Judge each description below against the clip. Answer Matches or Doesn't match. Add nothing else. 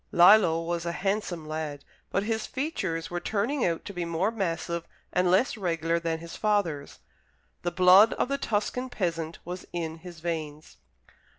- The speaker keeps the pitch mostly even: Doesn't match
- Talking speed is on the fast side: Doesn't match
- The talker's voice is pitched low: Doesn't match